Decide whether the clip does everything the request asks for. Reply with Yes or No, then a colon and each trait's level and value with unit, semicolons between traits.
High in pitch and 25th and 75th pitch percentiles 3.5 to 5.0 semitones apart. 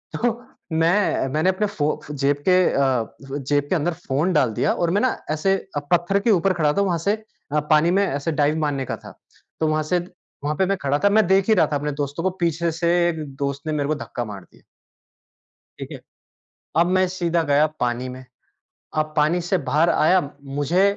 No: medium, 160 Hz; average, 4.1 semitones